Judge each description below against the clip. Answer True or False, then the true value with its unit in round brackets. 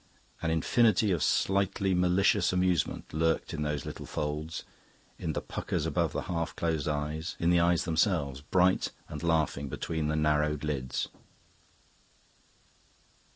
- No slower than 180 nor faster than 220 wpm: False (135 wpm)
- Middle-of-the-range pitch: False (80 Hz)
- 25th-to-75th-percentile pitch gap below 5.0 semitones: True (3.0 semitones)